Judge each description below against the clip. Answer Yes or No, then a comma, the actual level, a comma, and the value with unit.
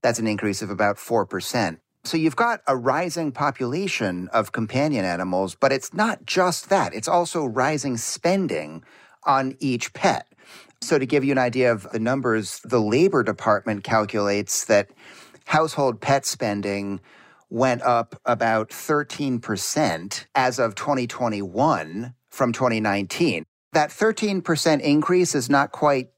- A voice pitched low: Yes, low, 130 Hz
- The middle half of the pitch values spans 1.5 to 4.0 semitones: No, wide, 5.6 semitones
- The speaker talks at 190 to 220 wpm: No, slow, 135 wpm